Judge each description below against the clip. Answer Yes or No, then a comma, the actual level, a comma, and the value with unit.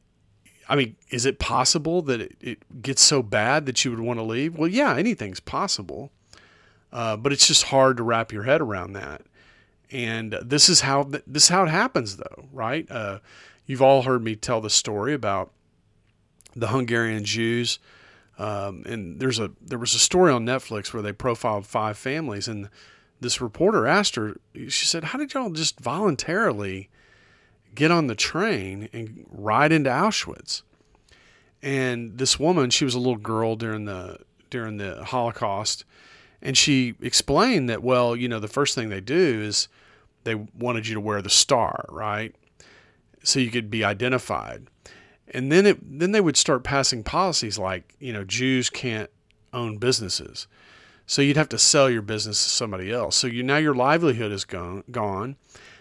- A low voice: Yes, low, 120 Hz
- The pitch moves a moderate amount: Yes, average, 4.2 semitones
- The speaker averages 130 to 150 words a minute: No, average, 175 wpm